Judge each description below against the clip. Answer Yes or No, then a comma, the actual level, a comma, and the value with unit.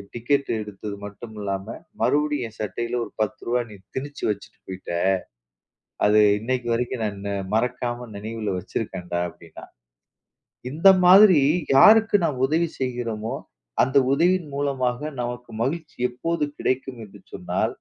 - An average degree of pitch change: Yes, average, 4.9 semitones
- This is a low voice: Yes, low, 120 Hz